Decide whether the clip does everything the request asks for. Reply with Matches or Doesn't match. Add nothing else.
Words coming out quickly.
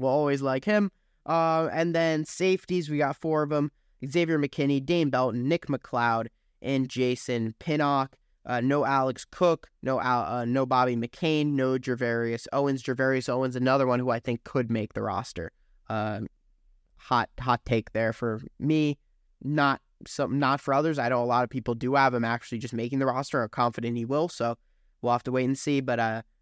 Doesn't match